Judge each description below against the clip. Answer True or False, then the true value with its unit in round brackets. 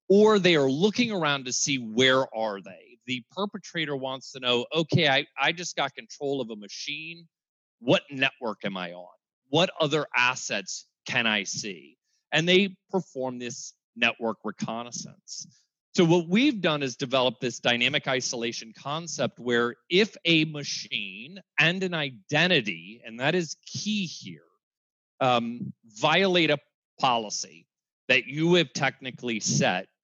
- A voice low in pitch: False (145 Hz)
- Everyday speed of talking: True (145 wpm)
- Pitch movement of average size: False (5.9 semitones)